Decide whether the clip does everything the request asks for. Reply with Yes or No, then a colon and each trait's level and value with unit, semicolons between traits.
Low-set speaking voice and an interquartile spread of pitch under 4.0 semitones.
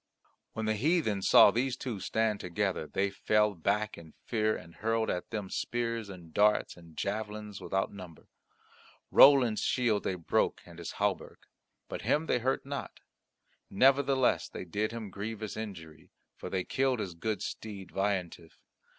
Yes: low, 105 Hz; average, 3.1 semitones